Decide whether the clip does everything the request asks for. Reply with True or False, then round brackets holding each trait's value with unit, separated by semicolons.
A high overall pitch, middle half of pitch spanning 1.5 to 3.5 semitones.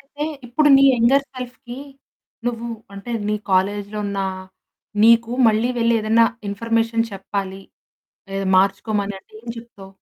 True (225 Hz; 2.9 semitones)